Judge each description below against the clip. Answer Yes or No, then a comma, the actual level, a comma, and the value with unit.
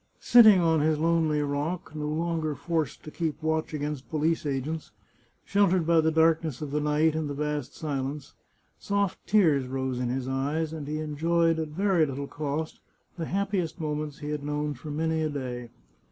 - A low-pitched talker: No, medium, 155 Hz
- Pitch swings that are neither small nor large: No, narrow, 2.0 semitones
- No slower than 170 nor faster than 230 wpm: Yes, average, 180 wpm